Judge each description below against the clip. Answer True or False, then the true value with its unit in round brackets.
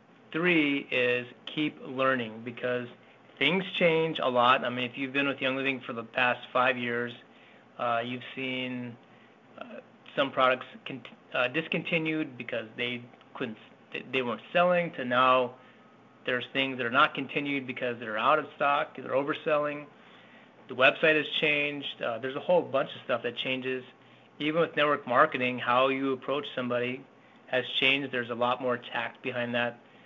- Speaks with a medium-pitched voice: False (130 Hz)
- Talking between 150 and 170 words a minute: True (165 wpm)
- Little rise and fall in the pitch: False (3.1 semitones)